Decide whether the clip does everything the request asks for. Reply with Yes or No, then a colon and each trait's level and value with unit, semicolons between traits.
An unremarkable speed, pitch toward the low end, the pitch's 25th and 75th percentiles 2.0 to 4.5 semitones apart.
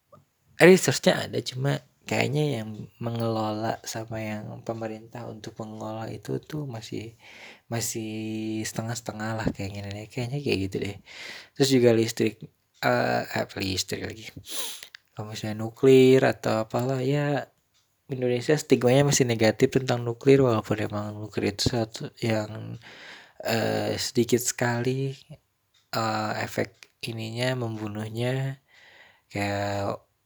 Yes: average, 115 wpm; low, 115 Hz; average, 3.0 semitones